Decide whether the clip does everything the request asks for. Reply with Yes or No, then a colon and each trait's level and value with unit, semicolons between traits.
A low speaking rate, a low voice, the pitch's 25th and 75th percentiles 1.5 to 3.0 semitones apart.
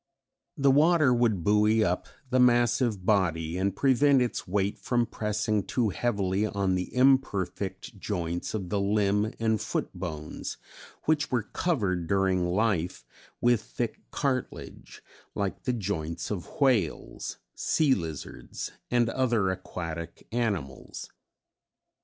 No: slow, 125 wpm; low, 105 Hz; average, 4.8 semitones